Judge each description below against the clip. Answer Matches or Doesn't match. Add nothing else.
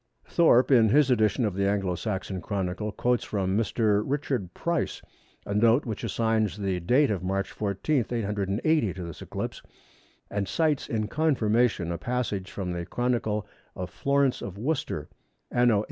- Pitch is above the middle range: Doesn't match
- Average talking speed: Matches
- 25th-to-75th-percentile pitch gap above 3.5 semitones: Matches